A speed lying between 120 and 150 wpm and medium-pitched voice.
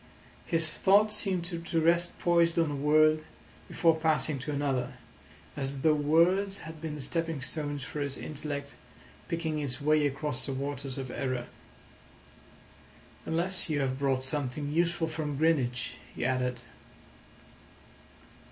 Yes: slow, 135 wpm; medium, 150 Hz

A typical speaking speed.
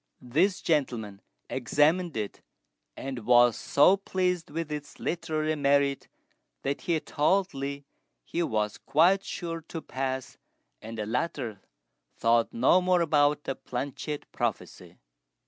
No: slow, 125 wpm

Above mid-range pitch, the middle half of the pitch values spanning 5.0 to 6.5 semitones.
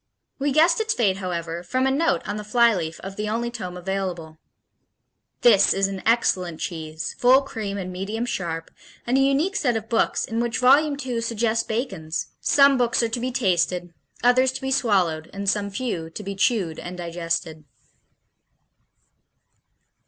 Yes: high, 210 Hz; wide, 5.6 semitones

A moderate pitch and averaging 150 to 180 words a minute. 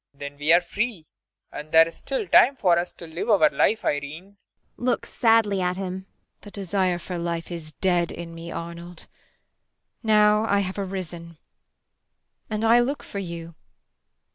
Yes: medium, 180 Hz; average, 165 wpm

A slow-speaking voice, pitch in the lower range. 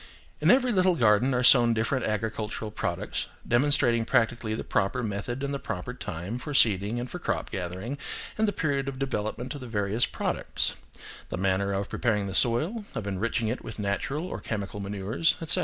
No: average, 185 wpm; low, 115 Hz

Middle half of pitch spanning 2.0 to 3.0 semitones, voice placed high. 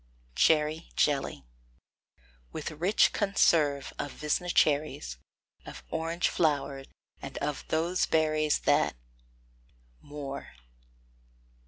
No: narrow, 2.4 semitones; medium, 150 Hz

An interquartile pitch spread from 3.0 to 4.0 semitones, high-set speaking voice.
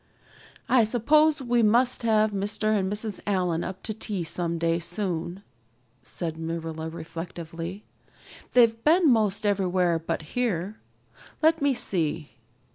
No: average, 5.3 semitones; high, 200 Hz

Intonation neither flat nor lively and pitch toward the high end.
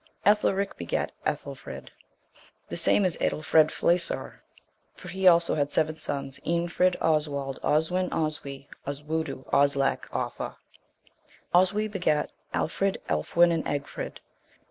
No: average, 3.9 semitones; medium, 160 Hz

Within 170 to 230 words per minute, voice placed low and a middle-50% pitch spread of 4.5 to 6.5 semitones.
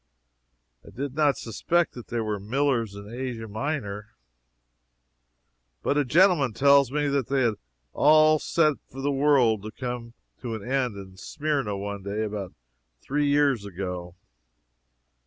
No: average, 150 wpm; low, 125 Hz; average, 5.3 semitones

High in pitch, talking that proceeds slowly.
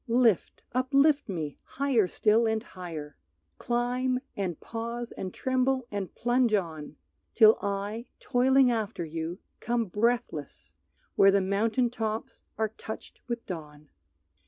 Yes: high, 220 Hz; slow, 125 wpm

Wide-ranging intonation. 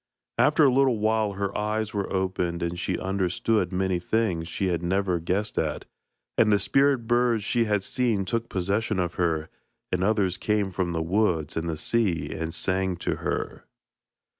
No: average, 3.9 semitones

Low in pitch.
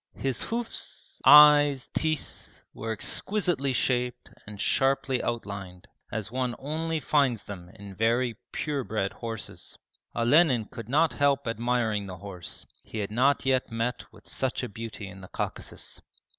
Yes: low, 120 Hz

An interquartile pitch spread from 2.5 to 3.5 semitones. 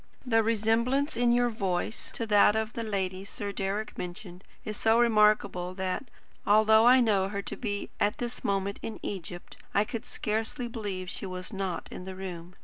Yes: average, 3.0 semitones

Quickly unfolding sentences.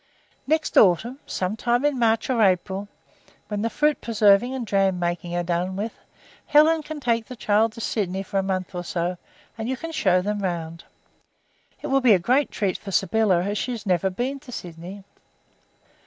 No: average, 190 wpm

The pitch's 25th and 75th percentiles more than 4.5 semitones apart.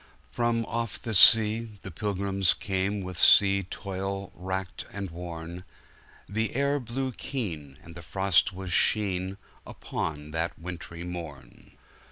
No: average, 3.4 semitones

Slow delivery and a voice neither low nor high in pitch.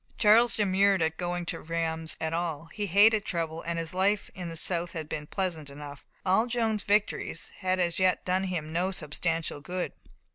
No: average, 185 wpm; medium, 175 Hz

